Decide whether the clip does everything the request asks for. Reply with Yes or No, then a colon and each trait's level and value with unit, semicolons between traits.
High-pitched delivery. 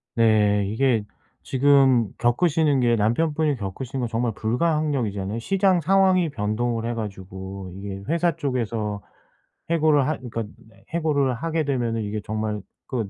No: low, 120 Hz